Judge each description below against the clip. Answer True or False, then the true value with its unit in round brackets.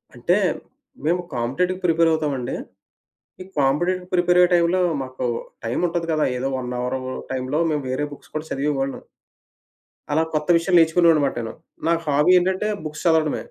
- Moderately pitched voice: True (155 Hz)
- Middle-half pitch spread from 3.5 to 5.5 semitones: True (4.3 semitones)